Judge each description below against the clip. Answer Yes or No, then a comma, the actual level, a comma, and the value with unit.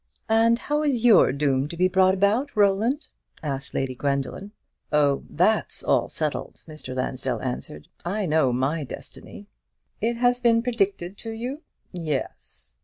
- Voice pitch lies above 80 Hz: Yes, medium, 185 Hz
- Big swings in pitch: Yes, wide, 8.6 semitones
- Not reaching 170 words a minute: Yes, average, 145 wpm